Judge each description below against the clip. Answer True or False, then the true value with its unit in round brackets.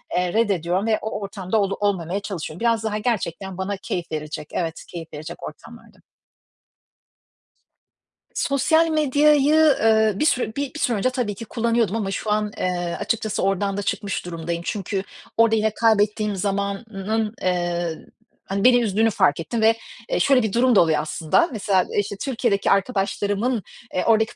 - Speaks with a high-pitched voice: True (205 Hz)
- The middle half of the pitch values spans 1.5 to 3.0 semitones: False (3.7 semitones)